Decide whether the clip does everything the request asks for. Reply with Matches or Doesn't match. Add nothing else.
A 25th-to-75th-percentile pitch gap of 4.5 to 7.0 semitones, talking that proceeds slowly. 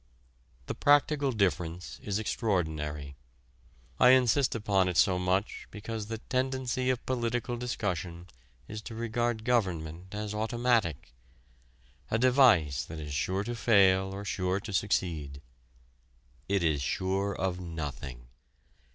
Matches